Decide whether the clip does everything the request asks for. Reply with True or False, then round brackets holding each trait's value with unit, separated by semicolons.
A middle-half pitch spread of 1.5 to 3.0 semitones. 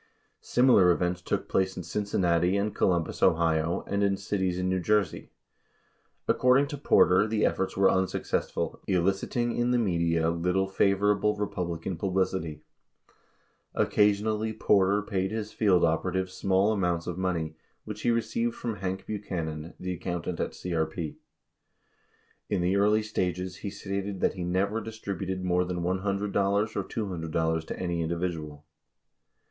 True (2.7 semitones)